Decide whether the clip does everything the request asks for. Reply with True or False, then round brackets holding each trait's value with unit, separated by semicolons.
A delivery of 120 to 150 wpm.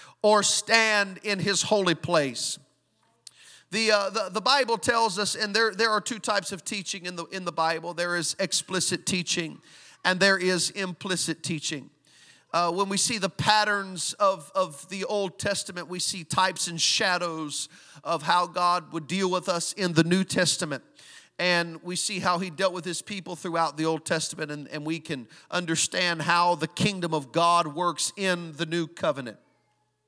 False (180 wpm)